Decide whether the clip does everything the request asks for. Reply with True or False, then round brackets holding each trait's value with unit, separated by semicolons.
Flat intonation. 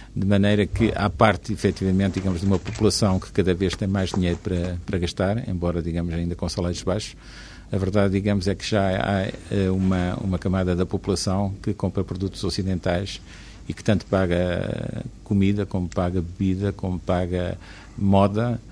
True (1.9 semitones)